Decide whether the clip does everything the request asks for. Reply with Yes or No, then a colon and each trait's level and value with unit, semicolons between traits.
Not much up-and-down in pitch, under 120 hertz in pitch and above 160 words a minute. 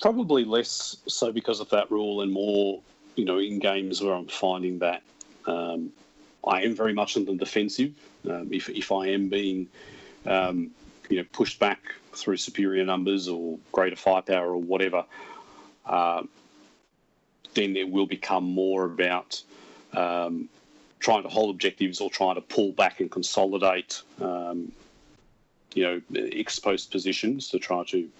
No: narrow, 2.0 semitones; very low, 95 Hz; average, 150 wpm